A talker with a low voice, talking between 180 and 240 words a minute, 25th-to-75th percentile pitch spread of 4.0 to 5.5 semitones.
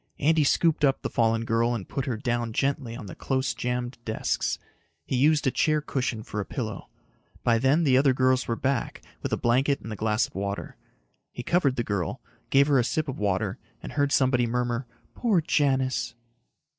No: low, 125 Hz; average, 195 wpm; average, 3.2 semitones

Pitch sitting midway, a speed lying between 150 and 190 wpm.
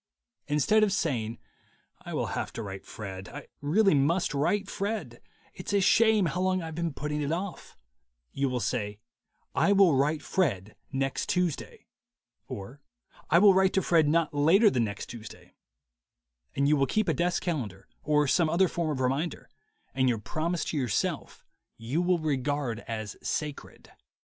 Yes: medium, 150 Hz; average, 165 wpm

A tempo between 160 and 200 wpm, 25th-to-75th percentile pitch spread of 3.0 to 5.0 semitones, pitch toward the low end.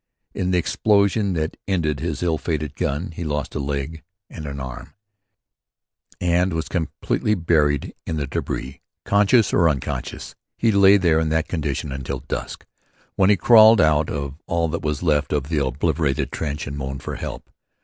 Yes: average, 170 wpm; average, 3.7 semitones; very low, 80 Hz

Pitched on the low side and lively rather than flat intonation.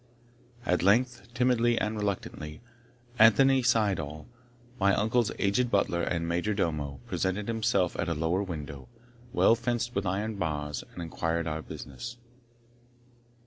Yes: low, 100 Hz; wide, 5.7 semitones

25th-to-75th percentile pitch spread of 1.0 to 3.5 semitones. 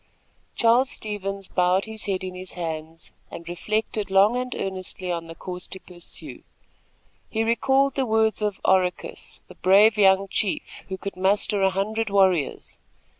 Yes: average, 3.0 semitones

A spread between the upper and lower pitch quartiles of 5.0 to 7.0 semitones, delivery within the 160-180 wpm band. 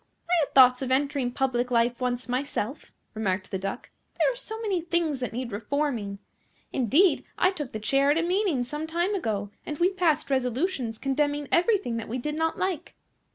No: wide, 5.4 semitones; average, 190 wpm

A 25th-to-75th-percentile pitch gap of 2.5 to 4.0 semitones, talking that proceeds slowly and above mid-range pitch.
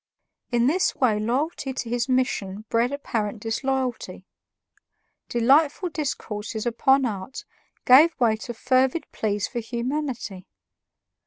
Yes: average, 3.4 semitones; slow, 110 wpm; high, 245 Hz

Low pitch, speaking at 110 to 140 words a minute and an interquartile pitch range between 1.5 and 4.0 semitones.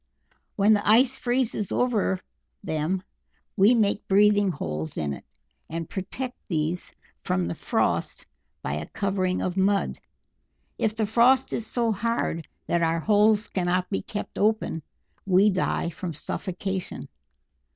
No: high, 195 Hz; slow, 135 wpm; average, 3.7 semitones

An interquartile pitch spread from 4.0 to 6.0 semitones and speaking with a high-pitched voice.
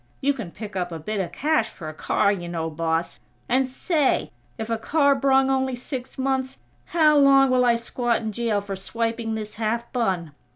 Yes: average, 5.0 semitones; high, 235 Hz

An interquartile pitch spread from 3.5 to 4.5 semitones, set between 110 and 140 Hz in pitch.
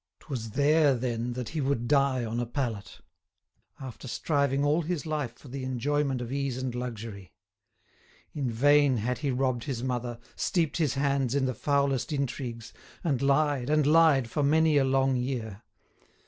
No: average, 2.9 semitones; low, 135 Hz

